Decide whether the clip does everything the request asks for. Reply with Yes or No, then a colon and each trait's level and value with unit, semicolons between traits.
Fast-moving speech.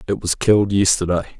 No: average, 170 wpm